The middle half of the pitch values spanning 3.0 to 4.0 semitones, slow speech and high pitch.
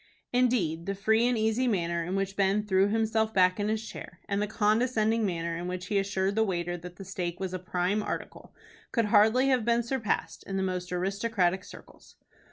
No: average, 3.3 semitones; average, 200 wpm; high, 200 Hz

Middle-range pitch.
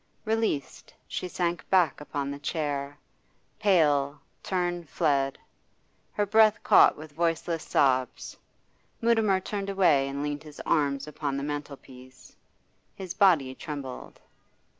Yes: medium, 150 Hz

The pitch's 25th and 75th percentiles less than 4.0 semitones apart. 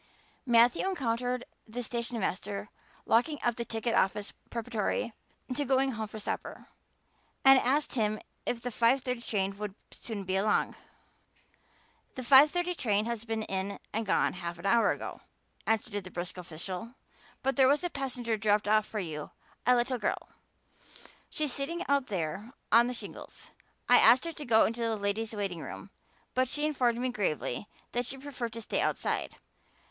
Yes: average, 3.6 semitones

